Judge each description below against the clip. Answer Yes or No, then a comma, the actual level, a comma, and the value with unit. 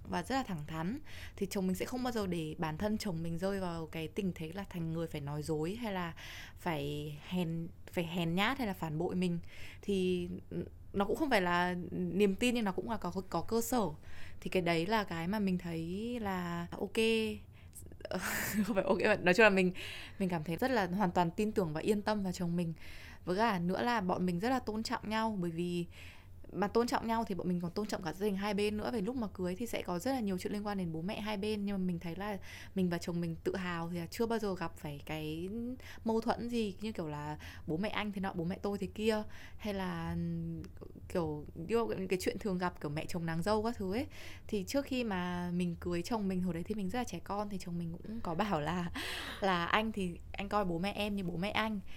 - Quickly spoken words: Yes, fast, 255 wpm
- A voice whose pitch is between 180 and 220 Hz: Yes, high, 190 Hz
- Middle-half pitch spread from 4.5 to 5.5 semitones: No, average, 3.9 semitones